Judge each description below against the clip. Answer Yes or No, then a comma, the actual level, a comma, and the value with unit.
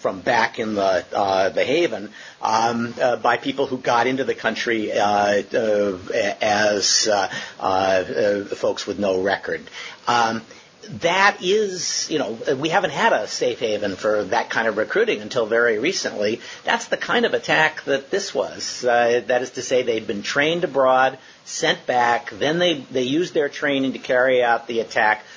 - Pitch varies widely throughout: Yes, wide, 5.9 semitones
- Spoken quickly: No, average, 175 wpm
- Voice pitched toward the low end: Yes, low, 125 Hz